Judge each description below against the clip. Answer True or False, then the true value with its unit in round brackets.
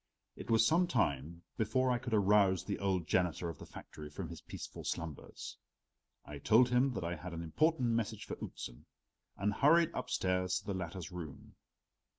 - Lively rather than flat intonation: True (5.8 semitones)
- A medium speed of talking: True (175 wpm)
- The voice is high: False (95 Hz)